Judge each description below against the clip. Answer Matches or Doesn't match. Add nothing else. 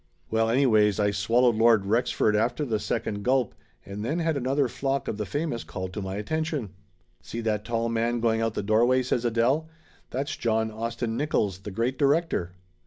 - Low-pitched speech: Matches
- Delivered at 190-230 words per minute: Matches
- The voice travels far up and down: Doesn't match